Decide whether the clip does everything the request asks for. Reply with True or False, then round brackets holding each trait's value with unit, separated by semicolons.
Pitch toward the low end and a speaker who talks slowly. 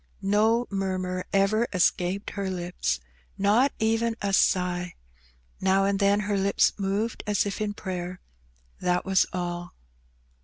False (195 Hz; 130 wpm)